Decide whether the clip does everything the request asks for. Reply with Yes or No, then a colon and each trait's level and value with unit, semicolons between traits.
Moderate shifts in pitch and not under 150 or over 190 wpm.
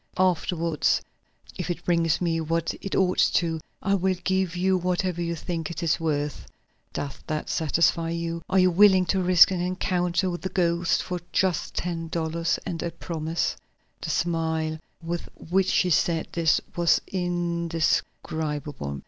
No: narrow, 1.8 semitones; average, 155 wpm